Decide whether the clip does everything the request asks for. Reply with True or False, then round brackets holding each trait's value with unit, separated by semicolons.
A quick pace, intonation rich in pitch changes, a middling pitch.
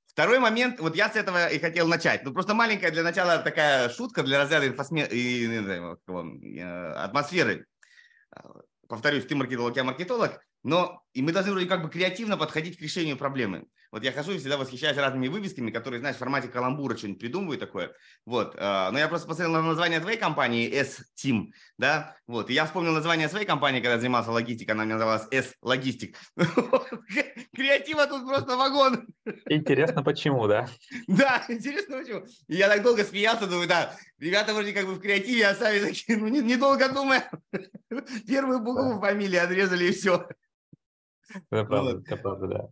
True (175 wpm; 8.4 semitones; 170 Hz)